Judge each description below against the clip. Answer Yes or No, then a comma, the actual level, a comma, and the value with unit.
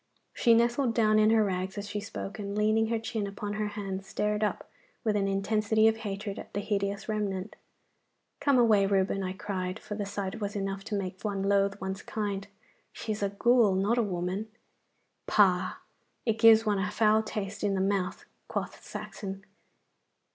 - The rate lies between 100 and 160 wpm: No, average, 185 wpm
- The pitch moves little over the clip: Yes, narrow, 1.8 semitones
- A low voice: No, high, 205 Hz